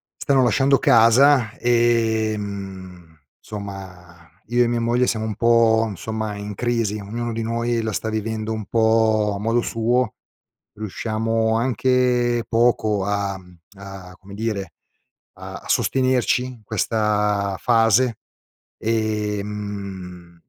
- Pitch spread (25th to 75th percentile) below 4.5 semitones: Yes, narrow, 2.6 semitones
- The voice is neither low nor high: No, low, 110 Hz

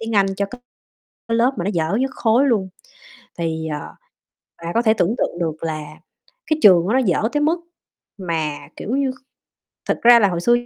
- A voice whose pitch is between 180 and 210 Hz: Yes, high, 200 Hz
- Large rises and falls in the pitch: Yes, wide, 6.1 semitones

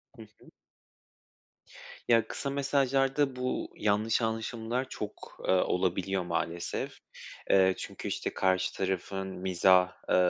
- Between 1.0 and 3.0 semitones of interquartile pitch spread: No, average, 5.3 semitones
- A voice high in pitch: No, low, 105 Hz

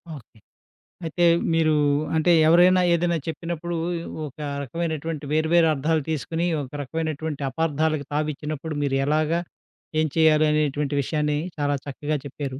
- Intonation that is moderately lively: No, narrow, 2.0 semitones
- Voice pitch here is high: No, medium, 155 Hz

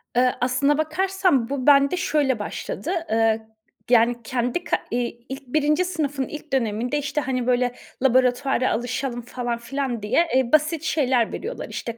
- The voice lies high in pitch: Yes, very high, 260 Hz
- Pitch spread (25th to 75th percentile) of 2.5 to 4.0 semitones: Yes, average, 3.5 semitones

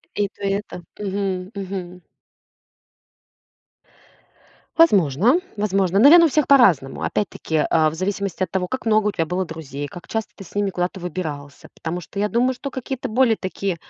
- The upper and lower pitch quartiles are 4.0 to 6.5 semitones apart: No, average, 3.5 semitones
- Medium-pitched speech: No, high, 195 Hz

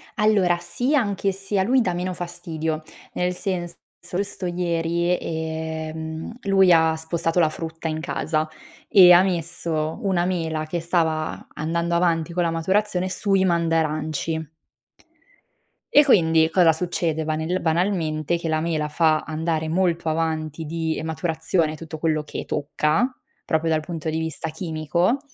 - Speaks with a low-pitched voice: No, medium, 165 Hz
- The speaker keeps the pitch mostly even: Yes, narrow, 2.1 semitones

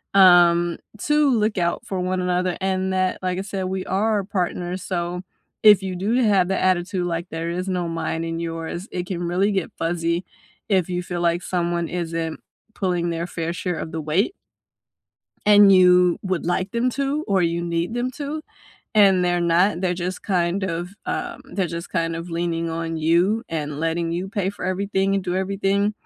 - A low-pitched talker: No, medium, 180 Hz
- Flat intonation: Yes, narrow, 2.2 semitones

